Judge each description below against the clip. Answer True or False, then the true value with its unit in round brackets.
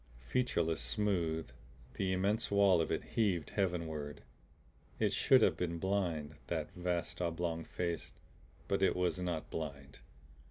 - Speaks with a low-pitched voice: True (85 Hz)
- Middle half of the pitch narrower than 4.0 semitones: True (3.0 semitones)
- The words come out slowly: True (130 wpm)